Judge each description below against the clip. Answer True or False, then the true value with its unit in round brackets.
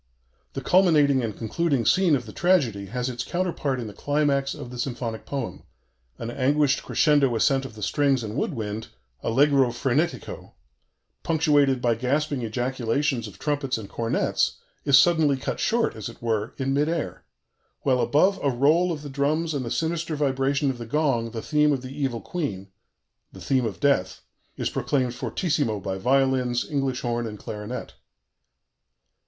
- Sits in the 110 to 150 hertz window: True (135 Hz)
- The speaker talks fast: False (165 wpm)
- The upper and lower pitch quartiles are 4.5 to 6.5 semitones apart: False (3.9 semitones)